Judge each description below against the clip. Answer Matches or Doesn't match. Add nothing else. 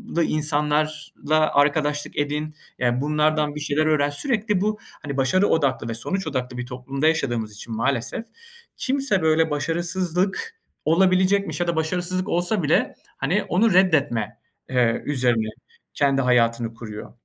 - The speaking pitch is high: Doesn't match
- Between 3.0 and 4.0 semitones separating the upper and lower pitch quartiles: Doesn't match